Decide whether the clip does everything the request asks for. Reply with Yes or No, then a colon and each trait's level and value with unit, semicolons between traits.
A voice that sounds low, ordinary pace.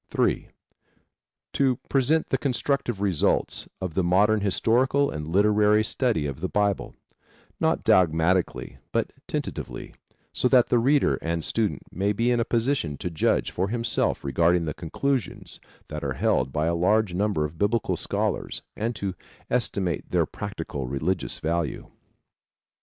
Yes: low, 100 Hz; average, 145 wpm